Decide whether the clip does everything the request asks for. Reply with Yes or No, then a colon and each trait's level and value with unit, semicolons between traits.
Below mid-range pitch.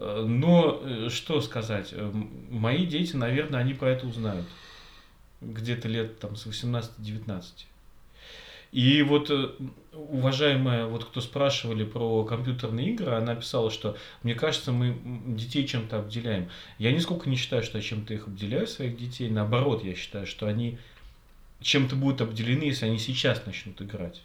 Yes: low, 115 Hz